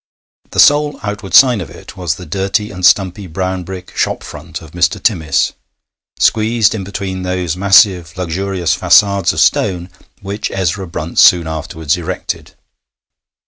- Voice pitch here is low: Yes, very low, 95 Hz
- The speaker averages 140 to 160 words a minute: Yes, average, 145 wpm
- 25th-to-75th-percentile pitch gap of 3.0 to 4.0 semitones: No, narrow, 2.6 semitones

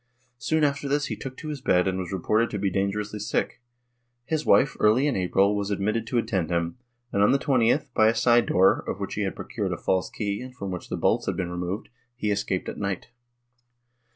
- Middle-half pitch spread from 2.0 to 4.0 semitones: No, average, 4.5 semitones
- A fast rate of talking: Yes, fast, 225 wpm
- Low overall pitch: Yes, low, 105 Hz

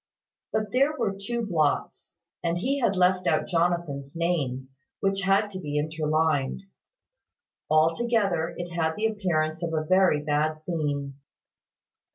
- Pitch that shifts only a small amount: No, average, 4.0 semitones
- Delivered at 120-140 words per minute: Yes, slow, 135 wpm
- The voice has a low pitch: No, medium, 170 Hz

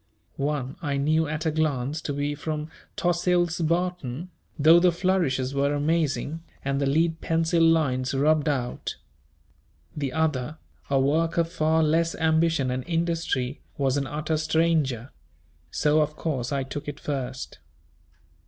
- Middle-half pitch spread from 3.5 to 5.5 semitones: No, average, 2.9 semitones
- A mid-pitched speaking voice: Yes, medium, 155 Hz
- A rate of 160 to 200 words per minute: No, average, 145 wpm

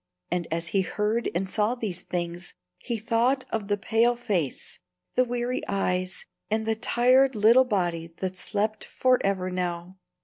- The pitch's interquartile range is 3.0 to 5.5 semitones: Yes, average, 4.6 semitones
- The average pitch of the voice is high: Yes, high, 210 Hz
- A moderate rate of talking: Yes, average, 150 wpm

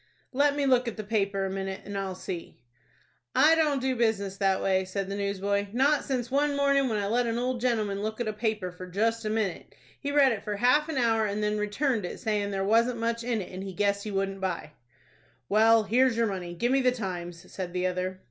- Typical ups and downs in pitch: Yes, average, 4.0 semitones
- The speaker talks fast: Yes, fast, 235 wpm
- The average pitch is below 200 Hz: No, high, 215 Hz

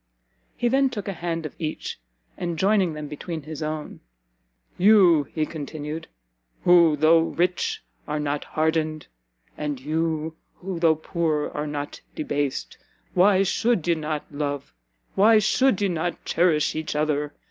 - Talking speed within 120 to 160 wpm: Yes, average, 145 wpm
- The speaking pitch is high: No, medium, 160 Hz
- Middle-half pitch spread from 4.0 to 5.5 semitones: No, average, 2.7 semitones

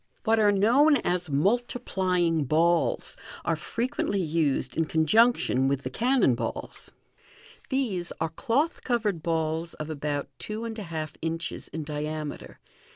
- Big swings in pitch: Yes, wide, 6.4 semitones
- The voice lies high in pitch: No, medium, 170 Hz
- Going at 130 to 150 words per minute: Yes, slow, 135 wpm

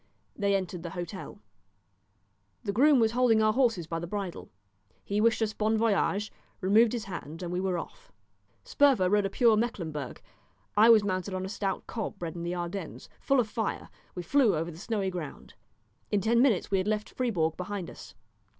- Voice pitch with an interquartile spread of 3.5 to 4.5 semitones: Yes, average, 4.0 semitones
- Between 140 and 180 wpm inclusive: No, average, 190 wpm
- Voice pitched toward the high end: Yes, high, 200 Hz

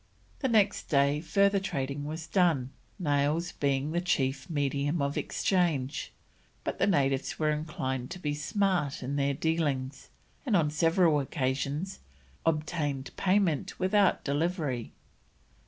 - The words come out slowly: Yes, slow, 125 wpm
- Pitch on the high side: No, medium, 150 Hz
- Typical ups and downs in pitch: Yes, average, 4.1 semitones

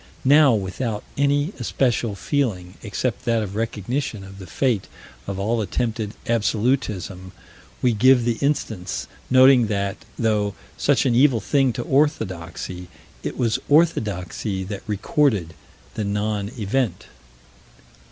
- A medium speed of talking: No, slow, 125 wpm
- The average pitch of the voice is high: No, low, 110 Hz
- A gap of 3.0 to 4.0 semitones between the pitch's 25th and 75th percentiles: No, average, 4.6 semitones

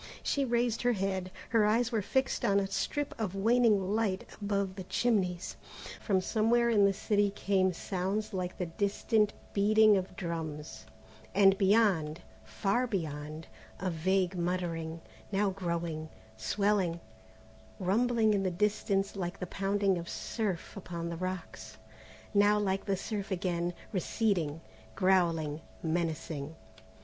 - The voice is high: Yes, high, 195 Hz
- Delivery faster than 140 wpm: No, slow, 135 wpm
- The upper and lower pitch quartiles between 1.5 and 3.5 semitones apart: Yes, average, 3.2 semitones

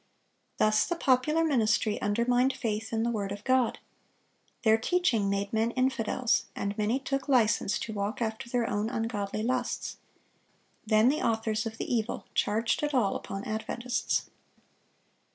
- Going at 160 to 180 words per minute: No, average, 150 wpm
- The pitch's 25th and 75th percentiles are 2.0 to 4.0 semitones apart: Yes, average, 2.8 semitones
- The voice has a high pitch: Yes, high, 225 Hz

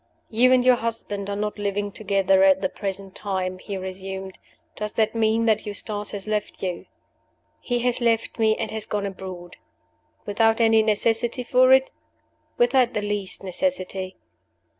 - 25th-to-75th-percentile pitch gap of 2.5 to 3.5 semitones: Yes, average, 2.9 semitones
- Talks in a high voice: Yes, high, 210 Hz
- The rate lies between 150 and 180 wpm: Yes, average, 160 wpm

